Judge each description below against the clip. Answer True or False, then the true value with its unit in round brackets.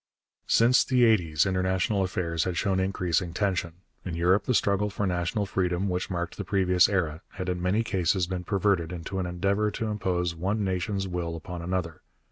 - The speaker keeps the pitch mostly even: True (2.2 semitones)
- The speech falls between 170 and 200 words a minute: True (180 wpm)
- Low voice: True (95 Hz)